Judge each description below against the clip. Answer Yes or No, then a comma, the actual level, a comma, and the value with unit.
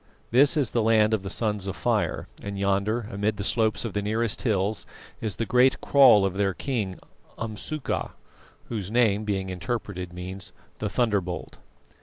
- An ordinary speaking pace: Yes, average, 165 wpm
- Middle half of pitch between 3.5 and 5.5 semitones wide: No, average, 2.9 semitones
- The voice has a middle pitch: No, low, 105 Hz